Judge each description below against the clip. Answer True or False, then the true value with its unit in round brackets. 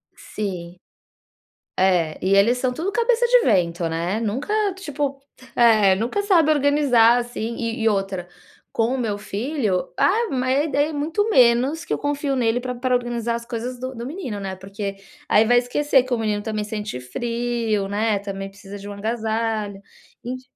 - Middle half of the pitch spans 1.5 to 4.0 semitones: False (4.7 semitones)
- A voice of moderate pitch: False (235 Hz)